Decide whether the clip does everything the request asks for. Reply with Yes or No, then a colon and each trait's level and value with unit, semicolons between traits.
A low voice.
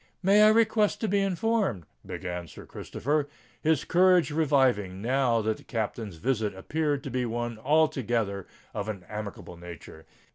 Yes: low, 125 Hz